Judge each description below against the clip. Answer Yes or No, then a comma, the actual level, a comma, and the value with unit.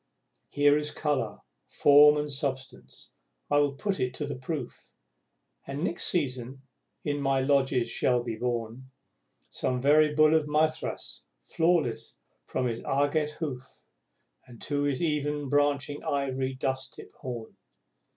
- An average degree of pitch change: No, narrow, 2.3 semitones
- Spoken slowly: Yes, slow, 130 wpm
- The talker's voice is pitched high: No, medium, 140 Hz